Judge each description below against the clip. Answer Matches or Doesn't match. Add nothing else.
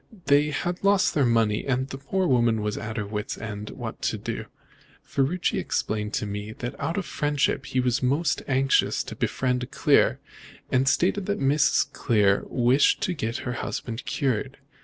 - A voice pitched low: Matches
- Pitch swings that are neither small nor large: Matches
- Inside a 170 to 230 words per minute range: Matches